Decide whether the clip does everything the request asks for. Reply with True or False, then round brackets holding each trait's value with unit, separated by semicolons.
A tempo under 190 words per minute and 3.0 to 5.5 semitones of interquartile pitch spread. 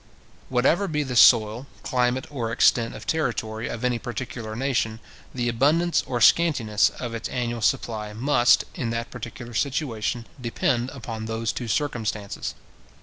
False (145 wpm; 2.6 semitones)